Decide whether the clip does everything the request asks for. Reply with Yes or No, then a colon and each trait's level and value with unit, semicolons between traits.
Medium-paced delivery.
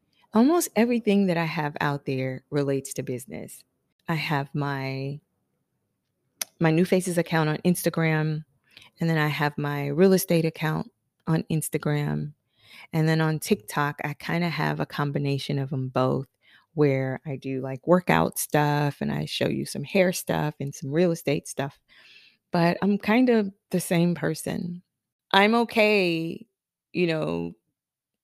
Yes: average, 150 wpm